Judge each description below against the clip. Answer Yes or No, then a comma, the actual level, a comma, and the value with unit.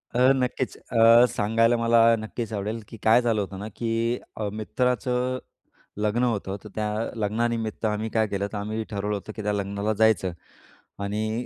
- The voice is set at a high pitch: No, low, 110 Hz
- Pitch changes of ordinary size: No, narrow, 2.0 semitones